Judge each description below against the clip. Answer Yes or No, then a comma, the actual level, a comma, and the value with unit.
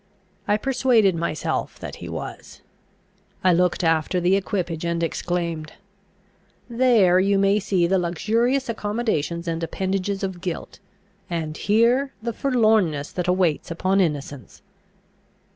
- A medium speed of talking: No, slow, 125 wpm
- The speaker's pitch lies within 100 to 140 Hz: No, medium, 185 Hz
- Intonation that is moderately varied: Yes, average, 4.2 semitones